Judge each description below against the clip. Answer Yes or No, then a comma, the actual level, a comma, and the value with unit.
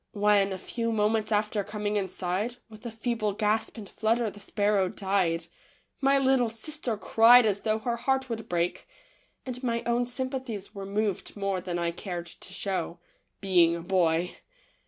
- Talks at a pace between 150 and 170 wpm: Yes, average, 165 wpm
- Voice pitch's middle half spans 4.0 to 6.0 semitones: No, average, 3.4 semitones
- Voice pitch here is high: Yes, high, 210 Hz